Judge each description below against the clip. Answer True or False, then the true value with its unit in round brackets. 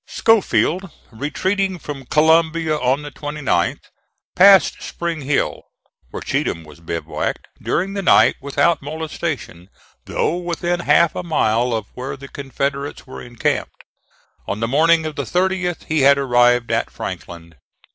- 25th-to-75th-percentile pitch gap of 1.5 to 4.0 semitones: False (5.3 semitones)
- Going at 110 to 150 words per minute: True (135 wpm)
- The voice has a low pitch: False (145 Hz)